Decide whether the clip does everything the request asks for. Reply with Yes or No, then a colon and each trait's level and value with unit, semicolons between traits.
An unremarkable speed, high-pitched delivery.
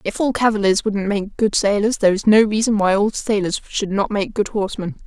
No: fast, 225 wpm; high, 205 Hz